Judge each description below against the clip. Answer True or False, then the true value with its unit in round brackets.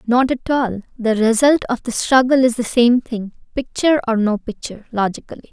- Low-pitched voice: False (240 Hz)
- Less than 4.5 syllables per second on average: False (5.4 syllables/s)